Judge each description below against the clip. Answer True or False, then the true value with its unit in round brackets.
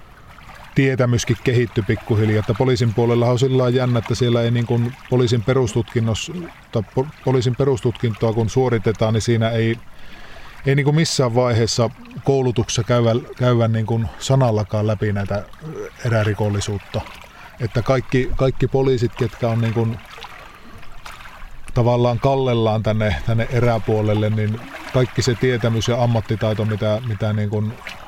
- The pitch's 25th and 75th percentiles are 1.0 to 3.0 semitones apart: True (2.4 semitones)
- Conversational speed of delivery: True (115 wpm)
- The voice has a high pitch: False (120 Hz)